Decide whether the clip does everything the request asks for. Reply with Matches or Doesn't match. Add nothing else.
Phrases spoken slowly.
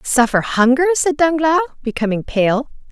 Matches